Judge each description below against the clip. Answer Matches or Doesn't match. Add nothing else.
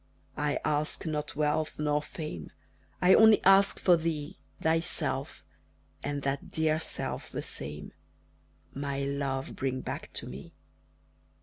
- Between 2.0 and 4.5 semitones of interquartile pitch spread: Matches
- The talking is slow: Matches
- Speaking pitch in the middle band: Matches